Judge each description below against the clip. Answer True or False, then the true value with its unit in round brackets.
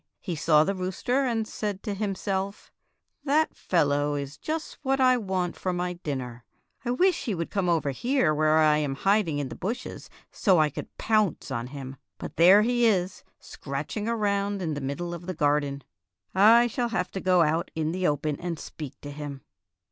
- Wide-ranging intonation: True (6.0 semitones)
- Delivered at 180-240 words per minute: True (195 wpm)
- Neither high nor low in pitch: True (180 Hz)